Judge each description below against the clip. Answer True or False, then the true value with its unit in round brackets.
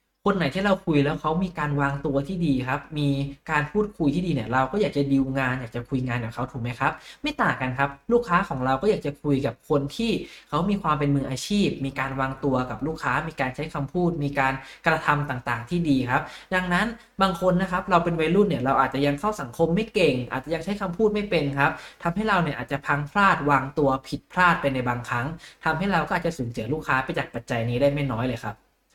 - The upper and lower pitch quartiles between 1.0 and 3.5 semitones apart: False (4.7 semitones)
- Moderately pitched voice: True (145 Hz)